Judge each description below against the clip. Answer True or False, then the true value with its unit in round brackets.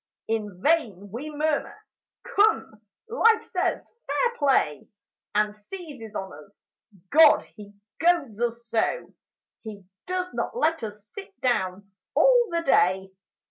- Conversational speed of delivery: False (125 wpm)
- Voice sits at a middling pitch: False (245 Hz)